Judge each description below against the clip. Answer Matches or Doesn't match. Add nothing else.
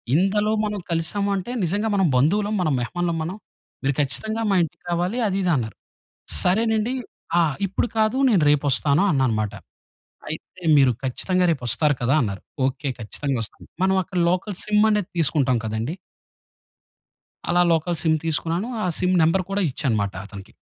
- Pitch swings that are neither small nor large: Doesn't match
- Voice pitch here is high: Doesn't match